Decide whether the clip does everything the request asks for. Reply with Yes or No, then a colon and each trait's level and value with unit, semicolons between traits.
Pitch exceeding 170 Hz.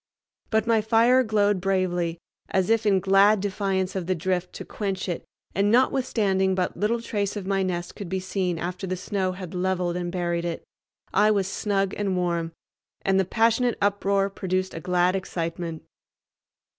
Yes: high, 190 Hz